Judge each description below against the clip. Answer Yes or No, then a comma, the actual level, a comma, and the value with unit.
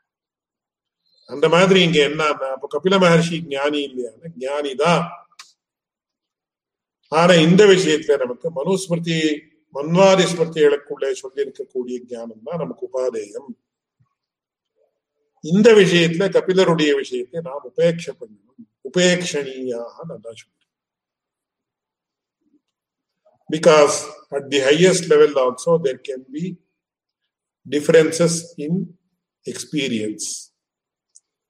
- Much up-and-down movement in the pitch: Yes, wide, 8.1 semitones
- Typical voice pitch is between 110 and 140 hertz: No, medium, 170 Hz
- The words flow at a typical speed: No, slow, 55 wpm